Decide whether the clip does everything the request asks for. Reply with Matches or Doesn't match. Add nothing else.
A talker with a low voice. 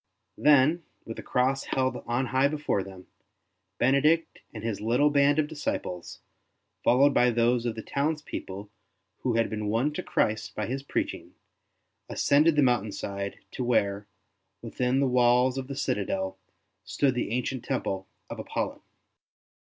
Matches